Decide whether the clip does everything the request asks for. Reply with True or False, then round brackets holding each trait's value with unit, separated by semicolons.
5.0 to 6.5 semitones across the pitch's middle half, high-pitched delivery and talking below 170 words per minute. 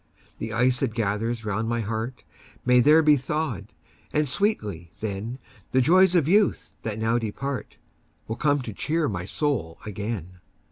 False (5.5 semitones; 120 Hz; 155 wpm)